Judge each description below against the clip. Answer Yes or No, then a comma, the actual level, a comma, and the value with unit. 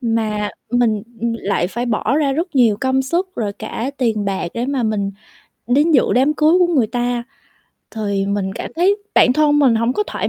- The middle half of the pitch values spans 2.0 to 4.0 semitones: No, average, 4.8 semitones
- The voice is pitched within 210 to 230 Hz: No, high, 245 Hz